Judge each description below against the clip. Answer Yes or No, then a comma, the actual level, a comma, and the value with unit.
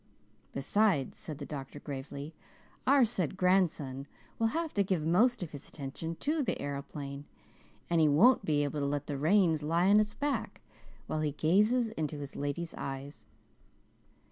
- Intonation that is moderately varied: No, wide, 6.1 semitones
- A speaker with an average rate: Yes, average, 160 wpm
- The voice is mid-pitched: Yes, medium, 155 Hz